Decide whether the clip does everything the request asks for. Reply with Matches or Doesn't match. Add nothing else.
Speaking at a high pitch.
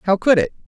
Matches